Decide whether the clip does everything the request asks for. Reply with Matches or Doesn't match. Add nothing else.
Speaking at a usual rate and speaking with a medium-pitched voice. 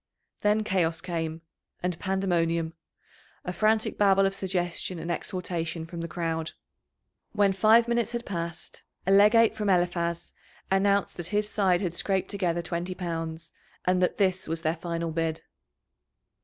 Matches